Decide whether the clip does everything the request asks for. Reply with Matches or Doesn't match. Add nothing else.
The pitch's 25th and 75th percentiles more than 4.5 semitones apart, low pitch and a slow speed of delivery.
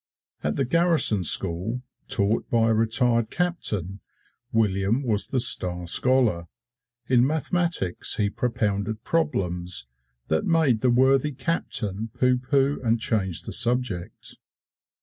Matches